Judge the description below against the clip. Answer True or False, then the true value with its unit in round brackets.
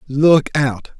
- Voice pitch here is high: False (140 Hz)